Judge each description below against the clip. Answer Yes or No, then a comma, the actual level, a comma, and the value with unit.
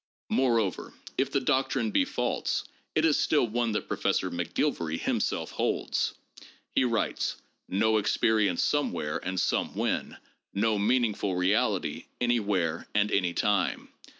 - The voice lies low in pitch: Yes, low, 110 Hz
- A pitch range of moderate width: Yes, average, 4.3 semitones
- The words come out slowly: Yes, slow, 120 wpm